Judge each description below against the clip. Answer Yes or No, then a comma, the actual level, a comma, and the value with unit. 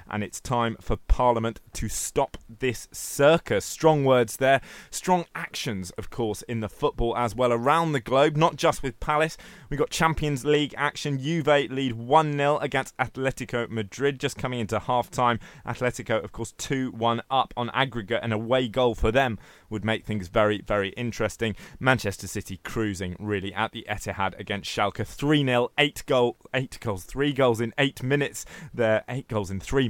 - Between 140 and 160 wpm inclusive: No, average, 175 wpm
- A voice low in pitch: Yes, low, 120 Hz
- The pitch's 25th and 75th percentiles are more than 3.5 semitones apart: Yes, average, 4.3 semitones